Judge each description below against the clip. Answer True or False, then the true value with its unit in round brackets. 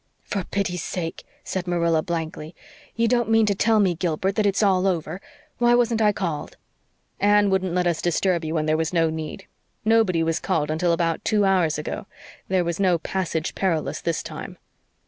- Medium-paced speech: True (185 wpm)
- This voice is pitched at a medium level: True (180 Hz)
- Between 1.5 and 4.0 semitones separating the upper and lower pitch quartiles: True (3.4 semitones)